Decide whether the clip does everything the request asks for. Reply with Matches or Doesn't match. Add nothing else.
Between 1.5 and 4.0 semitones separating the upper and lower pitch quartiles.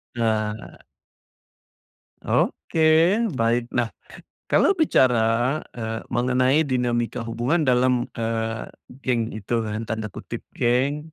Matches